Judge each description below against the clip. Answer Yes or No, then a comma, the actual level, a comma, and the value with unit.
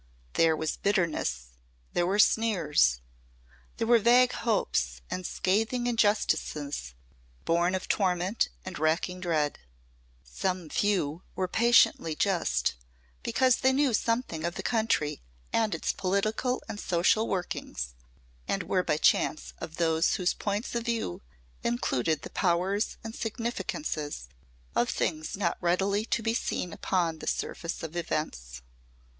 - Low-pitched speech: No, medium, 180 Hz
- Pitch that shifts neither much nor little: No, wide, 5.8 semitones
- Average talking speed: No, slow, 130 wpm